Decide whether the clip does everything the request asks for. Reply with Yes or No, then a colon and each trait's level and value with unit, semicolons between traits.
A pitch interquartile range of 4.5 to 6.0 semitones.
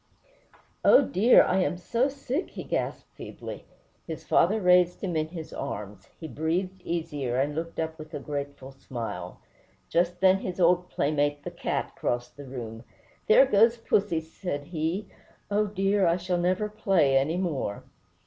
Yes: average, 4.8 semitones